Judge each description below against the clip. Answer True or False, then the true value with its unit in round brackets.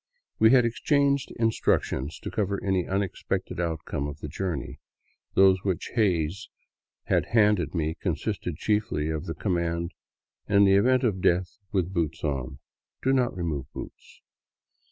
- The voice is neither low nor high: False (95 Hz)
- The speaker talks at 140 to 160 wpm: True (150 wpm)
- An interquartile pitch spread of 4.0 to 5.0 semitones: True (4.6 semitones)